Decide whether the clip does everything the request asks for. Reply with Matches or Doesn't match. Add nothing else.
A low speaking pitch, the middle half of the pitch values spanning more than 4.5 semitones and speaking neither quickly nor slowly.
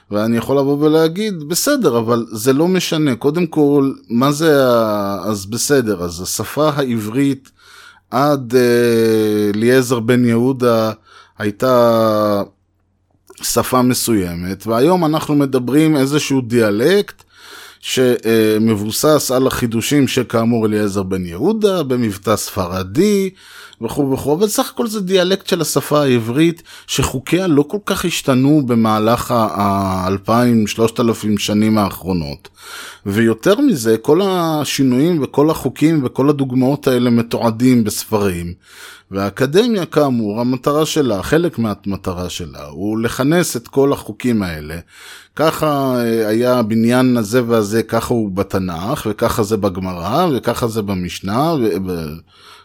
Matches